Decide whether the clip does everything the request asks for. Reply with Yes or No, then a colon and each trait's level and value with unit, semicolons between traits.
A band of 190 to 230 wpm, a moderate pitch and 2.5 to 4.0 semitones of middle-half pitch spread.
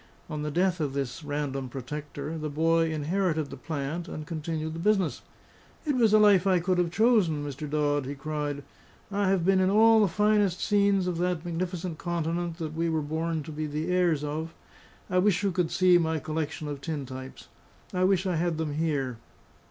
Yes: average, 200 wpm; medium, 165 Hz; average, 3.5 semitones